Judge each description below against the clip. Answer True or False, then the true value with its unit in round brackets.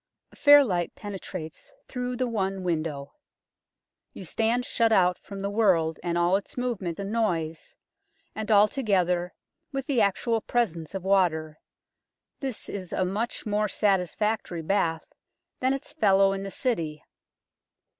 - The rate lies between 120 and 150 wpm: True (140 wpm)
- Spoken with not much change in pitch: False (4.5 semitones)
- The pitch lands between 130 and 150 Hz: False (195 Hz)